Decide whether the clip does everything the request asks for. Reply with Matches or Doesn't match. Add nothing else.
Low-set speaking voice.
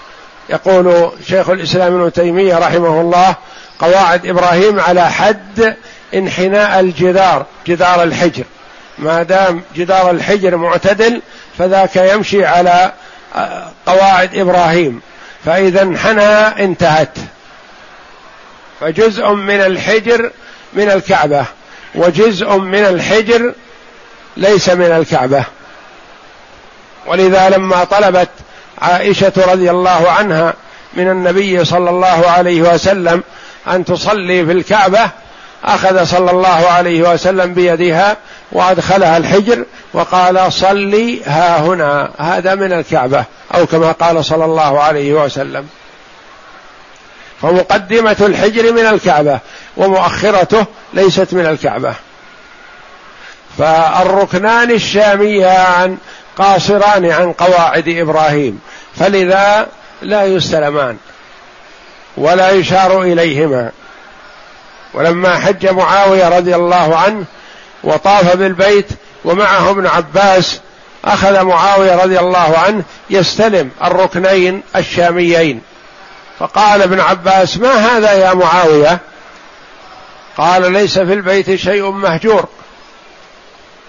Doesn't match